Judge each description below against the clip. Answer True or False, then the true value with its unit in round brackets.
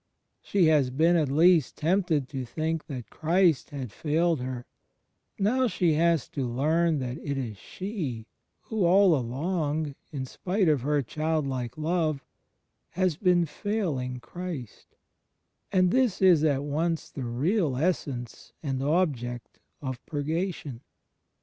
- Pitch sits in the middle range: True (155 Hz)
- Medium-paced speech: False (130 wpm)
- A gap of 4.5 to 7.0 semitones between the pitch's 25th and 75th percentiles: True (4.9 semitones)